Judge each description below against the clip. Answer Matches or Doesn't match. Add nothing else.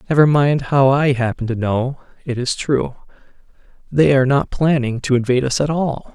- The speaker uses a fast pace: Doesn't match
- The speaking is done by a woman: Doesn't match